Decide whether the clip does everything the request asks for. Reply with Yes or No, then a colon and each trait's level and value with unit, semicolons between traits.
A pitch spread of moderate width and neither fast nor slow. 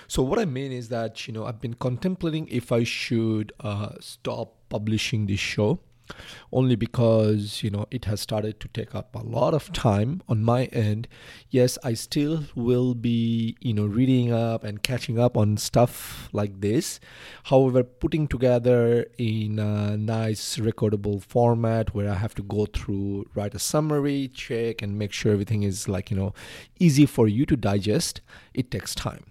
Yes: average, 3.1 semitones; average, 175 wpm